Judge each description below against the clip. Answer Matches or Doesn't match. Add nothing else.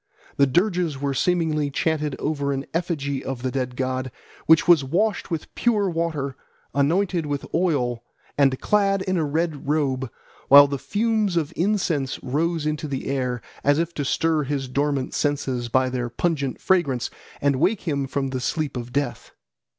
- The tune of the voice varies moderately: Matches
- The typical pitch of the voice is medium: Matches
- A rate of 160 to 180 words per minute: Matches